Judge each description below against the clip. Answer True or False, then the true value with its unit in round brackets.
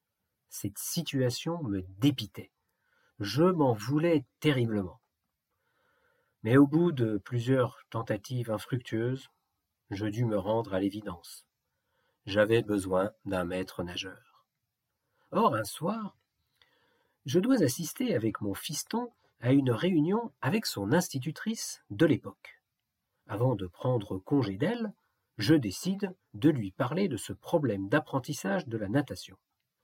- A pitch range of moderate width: False (6.9 semitones)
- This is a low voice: True (125 Hz)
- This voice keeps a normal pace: False (120 wpm)